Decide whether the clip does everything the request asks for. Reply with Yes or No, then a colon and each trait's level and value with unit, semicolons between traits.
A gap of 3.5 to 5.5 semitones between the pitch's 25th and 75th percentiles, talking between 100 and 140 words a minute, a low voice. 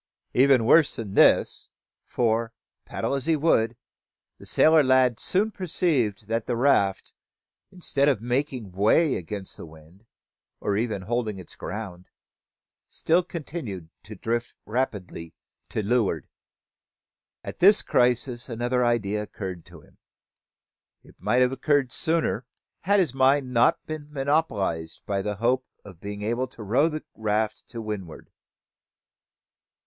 Yes: average, 5.1 semitones; slow, 135 wpm; low, 120 Hz